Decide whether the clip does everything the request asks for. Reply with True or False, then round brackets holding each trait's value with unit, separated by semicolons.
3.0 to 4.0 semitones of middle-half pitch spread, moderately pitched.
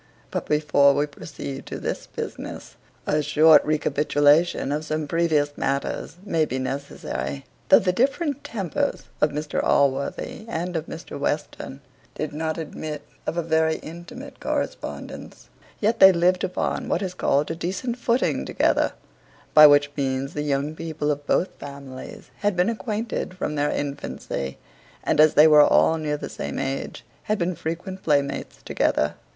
True (3.4 semitones; 155 Hz)